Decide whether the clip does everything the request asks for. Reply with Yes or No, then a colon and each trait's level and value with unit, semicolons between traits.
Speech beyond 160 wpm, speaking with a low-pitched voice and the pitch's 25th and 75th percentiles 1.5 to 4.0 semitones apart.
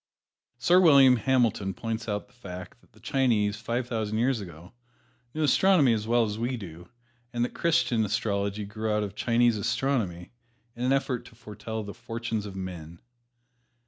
Yes: average, 170 wpm; low, 115 Hz; average, 3.2 semitones